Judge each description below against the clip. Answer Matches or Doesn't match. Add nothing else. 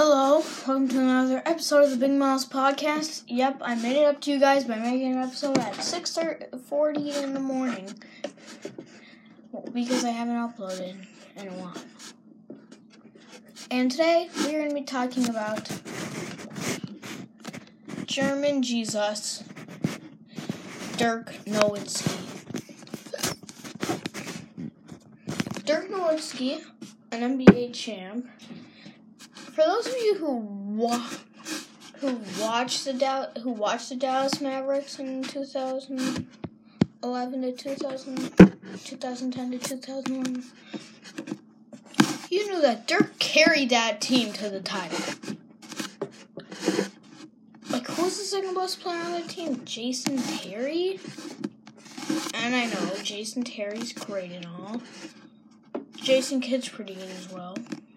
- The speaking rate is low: Matches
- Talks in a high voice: Matches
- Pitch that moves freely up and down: Doesn't match